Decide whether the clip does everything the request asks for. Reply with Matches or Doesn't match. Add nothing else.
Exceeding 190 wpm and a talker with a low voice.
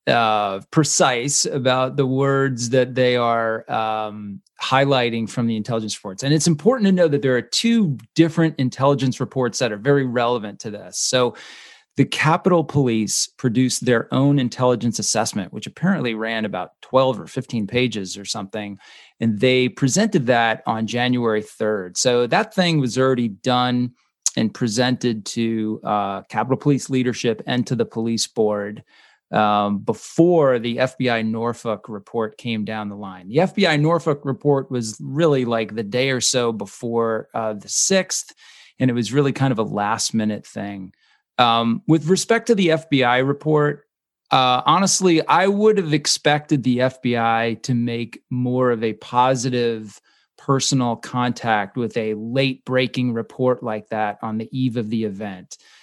Doesn't match